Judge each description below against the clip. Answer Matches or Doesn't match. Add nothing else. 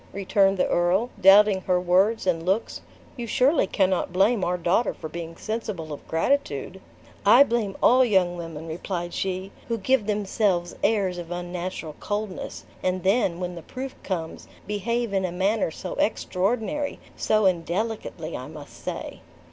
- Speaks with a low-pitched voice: Doesn't match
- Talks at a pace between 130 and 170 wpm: Matches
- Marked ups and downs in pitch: Doesn't match